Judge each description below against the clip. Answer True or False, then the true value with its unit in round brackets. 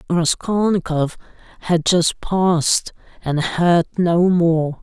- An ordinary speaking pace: False (100 wpm)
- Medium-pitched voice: True (170 Hz)